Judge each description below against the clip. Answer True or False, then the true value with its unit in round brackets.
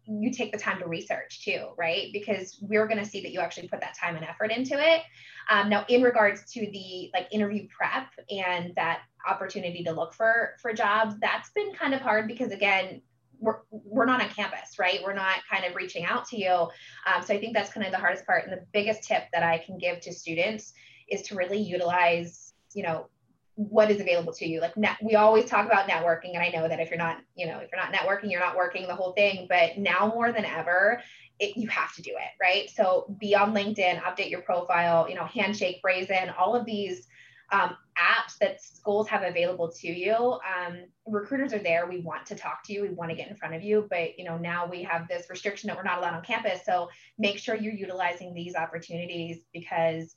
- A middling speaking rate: False (230 wpm)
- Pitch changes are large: False (3.6 semitones)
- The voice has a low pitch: False (190 Hz)